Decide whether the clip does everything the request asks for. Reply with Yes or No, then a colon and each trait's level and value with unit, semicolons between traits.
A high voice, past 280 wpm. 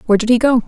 Yes: high, 235 Hz; fast, 360 wpm